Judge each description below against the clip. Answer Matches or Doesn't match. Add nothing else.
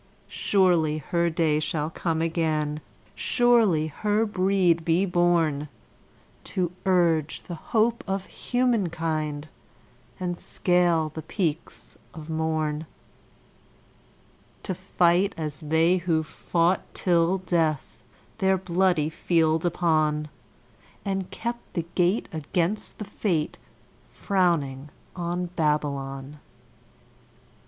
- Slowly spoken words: Matches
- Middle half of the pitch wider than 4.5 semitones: Doesn't match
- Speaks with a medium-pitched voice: Matches